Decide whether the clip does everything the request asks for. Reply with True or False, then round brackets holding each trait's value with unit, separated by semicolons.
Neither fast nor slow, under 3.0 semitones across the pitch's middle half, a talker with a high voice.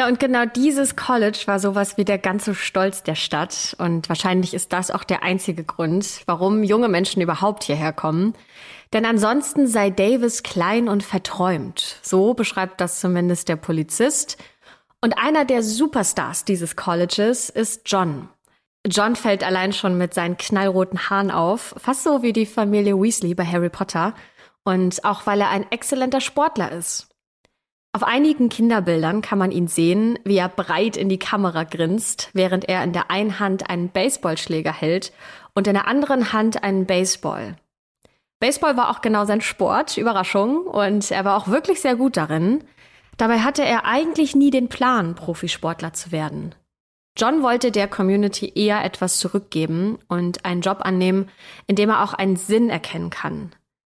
False (165 wpm; 4.0 semitones; 200 Hz)